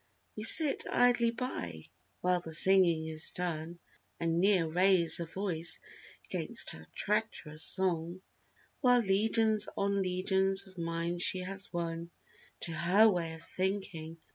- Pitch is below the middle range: No, medium, 180 Hz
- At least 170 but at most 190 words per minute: No, slow, 135 wpm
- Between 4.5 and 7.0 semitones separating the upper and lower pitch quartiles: No, average, 3.1 semitones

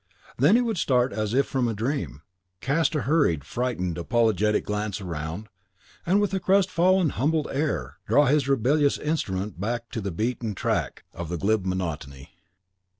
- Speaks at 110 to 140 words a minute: No, average, 160 wpm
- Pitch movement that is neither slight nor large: No, wide, 7.8 semitones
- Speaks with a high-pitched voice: No, low, 120 Hz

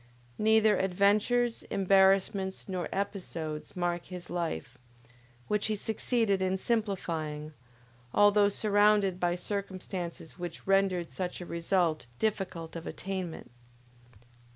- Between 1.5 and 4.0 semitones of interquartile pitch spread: Yes, average, 2.7 semitones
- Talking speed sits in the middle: No, slow, 105 wpm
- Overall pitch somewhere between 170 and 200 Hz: Yes, high, 190 Hz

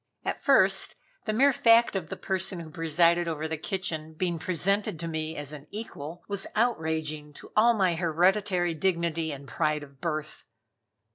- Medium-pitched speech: Yes, medium, 170 Hz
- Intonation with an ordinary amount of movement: Yes, average, 3.5 semitones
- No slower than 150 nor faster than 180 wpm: Yes, average, 165 wpm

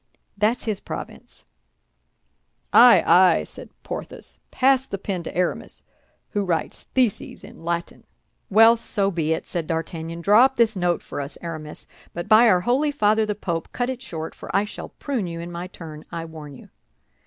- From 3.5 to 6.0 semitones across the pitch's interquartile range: Yes, average, 5.0 semitones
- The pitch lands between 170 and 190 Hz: Yes, medium, 185 Hz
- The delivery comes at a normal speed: Yes, average, 175 wpm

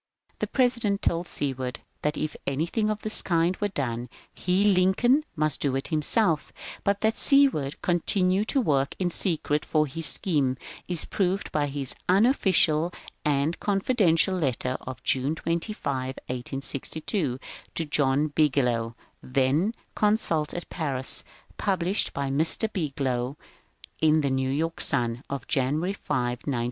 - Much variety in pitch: Yes, wide, 5.7 semitones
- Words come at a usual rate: Yes, average, 145 wpm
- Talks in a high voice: No, medium, 155 Hz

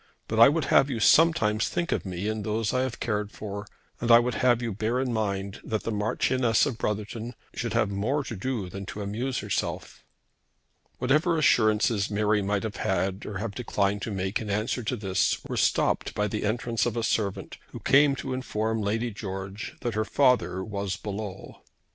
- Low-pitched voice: Yes, low, 110 Hz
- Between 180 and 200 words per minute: Yes, average, 195 wpm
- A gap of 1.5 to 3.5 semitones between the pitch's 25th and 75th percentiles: Yes, average, 3.1 semitones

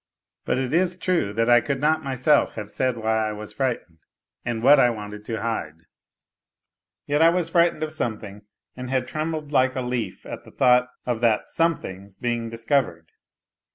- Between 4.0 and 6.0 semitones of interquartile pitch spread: Yes, average, 4.9 semitones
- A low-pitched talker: Yes, low, 125 Hz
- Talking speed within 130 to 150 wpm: No, average, 180 wpm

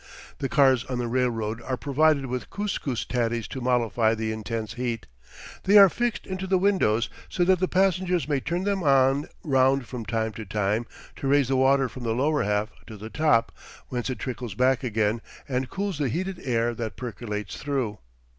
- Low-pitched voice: Yes, low, 125 Hz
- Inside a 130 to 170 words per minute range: No, average, 190 wpm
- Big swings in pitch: No, average, 4.8 semitones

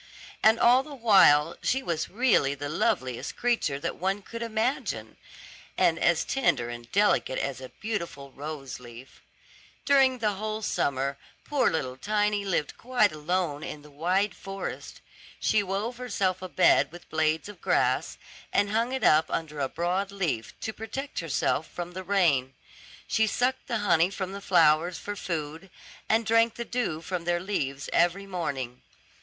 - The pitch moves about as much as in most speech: No, wide, 6.2 semitones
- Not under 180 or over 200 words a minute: No, average, 160 wpm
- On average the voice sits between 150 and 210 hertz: Yes, medium, 185 Hz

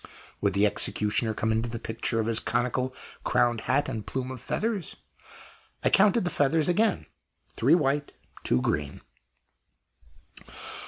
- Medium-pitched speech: No, low, 120 Hz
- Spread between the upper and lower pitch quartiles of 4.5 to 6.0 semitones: Yes, average, 4.9 semitones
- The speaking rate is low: Yes, slow, 130 wpm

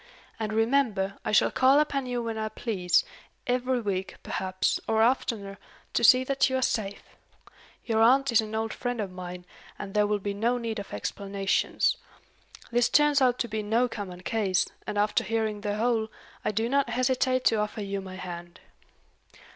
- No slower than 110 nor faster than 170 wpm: No, average, 180 wpm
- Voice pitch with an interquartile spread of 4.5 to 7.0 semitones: No, average, 3.6 semitones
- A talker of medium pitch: No, high, 220 Hz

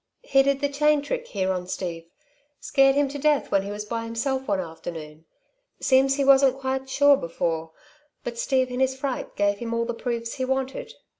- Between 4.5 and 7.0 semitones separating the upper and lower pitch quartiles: Yes, average, 5.2 semitones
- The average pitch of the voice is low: No, very high, 260 Hz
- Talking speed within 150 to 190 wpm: No, average, 200 wpm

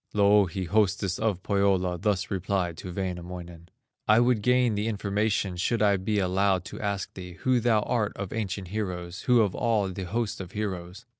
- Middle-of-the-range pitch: No, low, 100 Hz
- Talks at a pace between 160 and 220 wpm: Yes, average, 175 wpm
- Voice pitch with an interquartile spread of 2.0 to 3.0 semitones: Yes, average, 2.7 semitones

